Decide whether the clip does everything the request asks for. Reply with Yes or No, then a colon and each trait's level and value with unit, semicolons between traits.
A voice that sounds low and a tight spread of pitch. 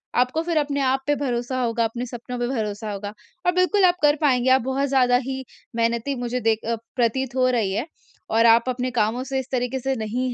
No: very high, 250 Hz; narrow, 2.3 semitones